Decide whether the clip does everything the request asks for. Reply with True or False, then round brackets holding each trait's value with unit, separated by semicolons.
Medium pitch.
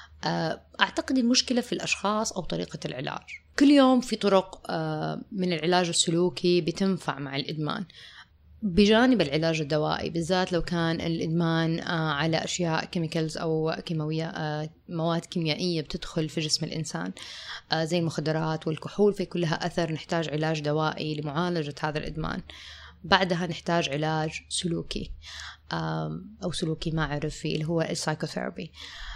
True (165 Hz)